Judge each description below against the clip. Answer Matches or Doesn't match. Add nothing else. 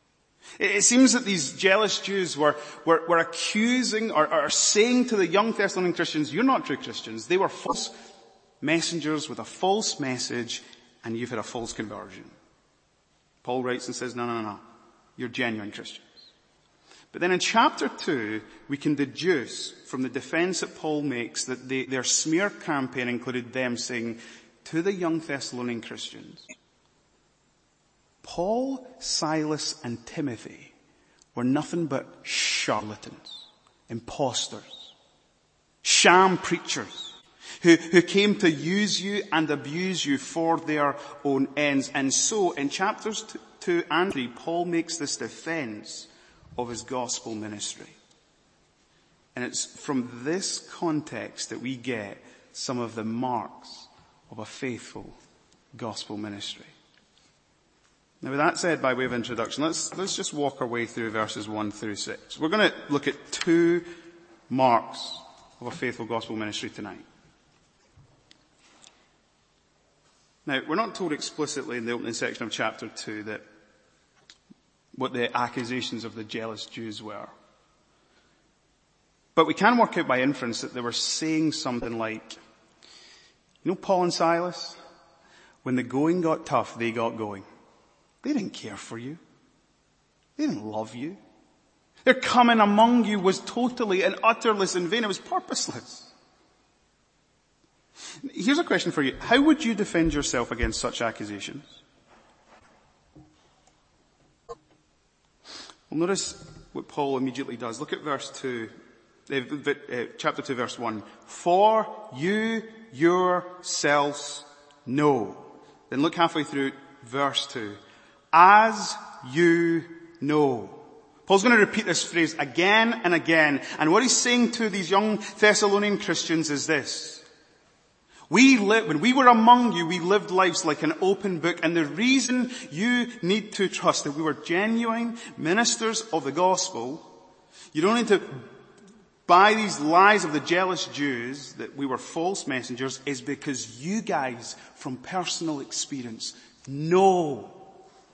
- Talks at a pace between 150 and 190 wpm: Doesn't match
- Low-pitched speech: Doesn't match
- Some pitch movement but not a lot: Doesn't match